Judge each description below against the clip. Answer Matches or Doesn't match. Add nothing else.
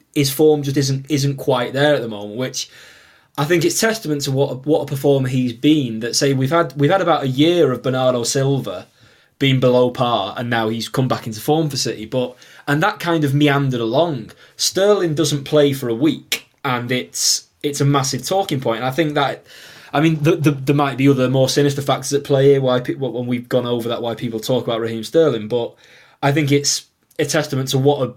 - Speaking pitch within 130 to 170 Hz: Matches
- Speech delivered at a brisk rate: Matches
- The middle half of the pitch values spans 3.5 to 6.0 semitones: Doesn't match